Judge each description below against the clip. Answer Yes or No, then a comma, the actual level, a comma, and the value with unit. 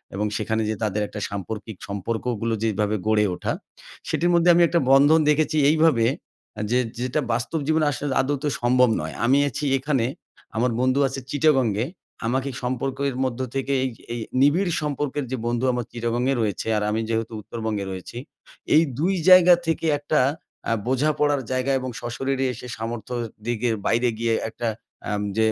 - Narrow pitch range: No, average, 4.2 semitones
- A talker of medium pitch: No, low, 125 Hz